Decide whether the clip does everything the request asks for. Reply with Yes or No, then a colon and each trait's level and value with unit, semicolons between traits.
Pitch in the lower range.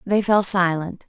No: medium, 185 Hz